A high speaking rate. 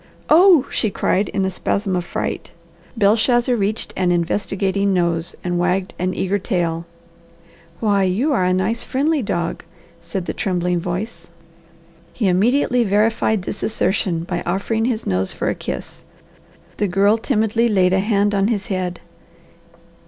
No: average, 150 wpm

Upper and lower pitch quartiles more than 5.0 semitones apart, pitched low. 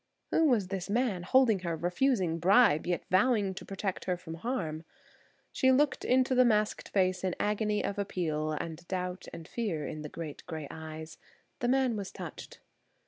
No: wide, 5.5 semitones; high, 190 Hz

